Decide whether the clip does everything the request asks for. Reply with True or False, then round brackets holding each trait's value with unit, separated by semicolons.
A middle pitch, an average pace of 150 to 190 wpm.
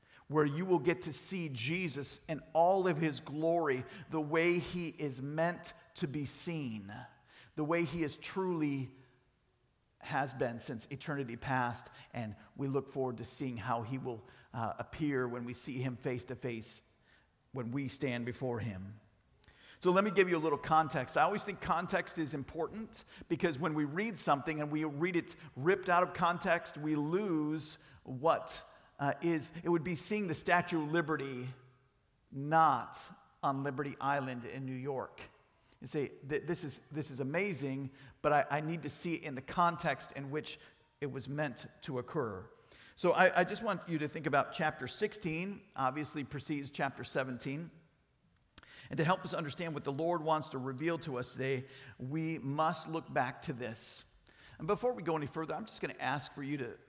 True (150 Hz; 180 wpm)